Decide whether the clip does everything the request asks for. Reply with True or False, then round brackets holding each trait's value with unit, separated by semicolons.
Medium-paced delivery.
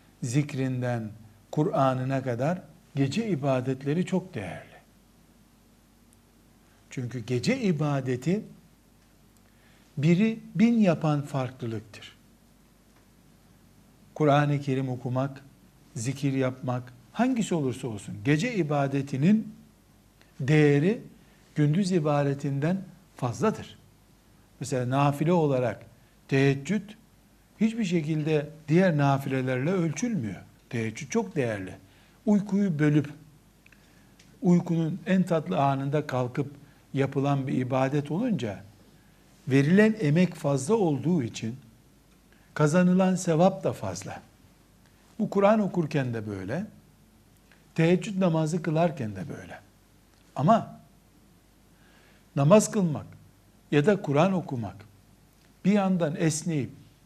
False (85 wpm)